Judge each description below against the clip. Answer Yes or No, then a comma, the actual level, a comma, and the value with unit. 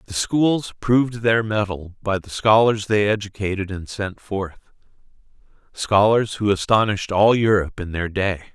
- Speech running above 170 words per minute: No, average, 150 wpm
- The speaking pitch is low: Yes, low, 100 Hz